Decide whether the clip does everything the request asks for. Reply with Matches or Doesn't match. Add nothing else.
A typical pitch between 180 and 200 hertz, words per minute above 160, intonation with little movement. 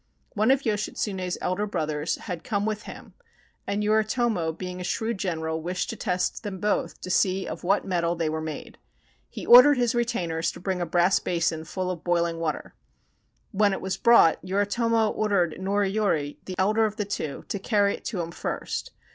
Doesn't match